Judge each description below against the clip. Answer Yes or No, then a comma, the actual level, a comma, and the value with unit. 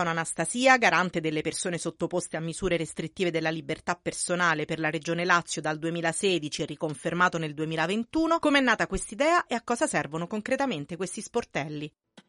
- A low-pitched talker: No, medium, 170 Hz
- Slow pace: No, average, 145 wpm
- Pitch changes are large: No, average, 4.6 semitones